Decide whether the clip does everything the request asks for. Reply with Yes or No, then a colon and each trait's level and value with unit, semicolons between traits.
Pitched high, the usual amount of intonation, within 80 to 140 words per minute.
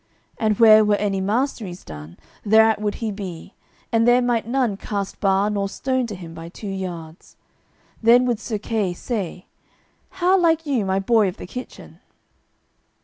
No: high, 210 Hz; average, 3.8 semitones; average, 165 wpm